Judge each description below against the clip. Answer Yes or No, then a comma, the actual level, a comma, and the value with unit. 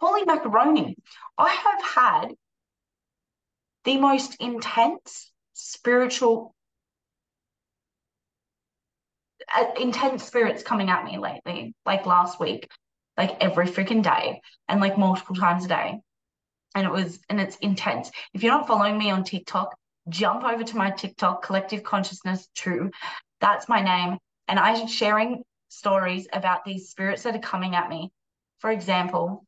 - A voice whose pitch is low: No, high, 200 Hz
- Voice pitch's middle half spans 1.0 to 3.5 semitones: No, average, 3.9 semitones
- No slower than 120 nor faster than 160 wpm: Yes, slow, 135 wpm